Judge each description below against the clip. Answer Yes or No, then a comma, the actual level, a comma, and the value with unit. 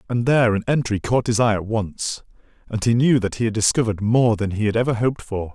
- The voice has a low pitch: Yes, low, 115 Hz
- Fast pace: Yes, fast, 240 wpm